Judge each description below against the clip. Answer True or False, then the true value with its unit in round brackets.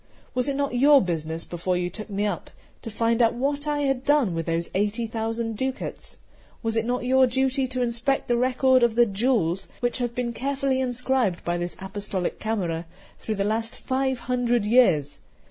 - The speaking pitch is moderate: False (235 Hz)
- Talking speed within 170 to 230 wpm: True (190 wpm)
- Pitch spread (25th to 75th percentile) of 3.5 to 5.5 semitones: True (4.5 semitones)